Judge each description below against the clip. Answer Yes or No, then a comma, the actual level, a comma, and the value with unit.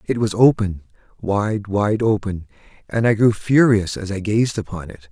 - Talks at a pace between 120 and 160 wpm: Yes, average, 150 wpm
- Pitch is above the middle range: No, low, 105 Hz